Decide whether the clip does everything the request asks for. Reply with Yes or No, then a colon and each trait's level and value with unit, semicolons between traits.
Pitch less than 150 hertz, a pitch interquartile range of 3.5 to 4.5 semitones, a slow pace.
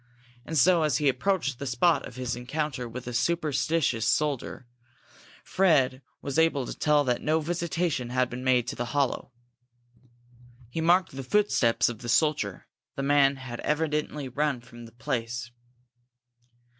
No: low, 135 Hz; average, 4.0 semitones; average, 155 wpm